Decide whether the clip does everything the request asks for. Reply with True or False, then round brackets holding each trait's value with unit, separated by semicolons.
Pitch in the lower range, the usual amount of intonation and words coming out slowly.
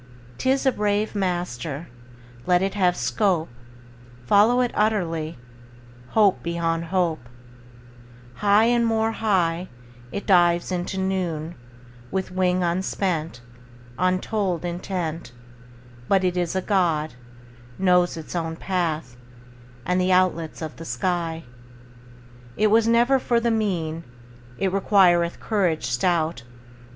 False (180 Hz; 3.4 semitones; 115 wpm)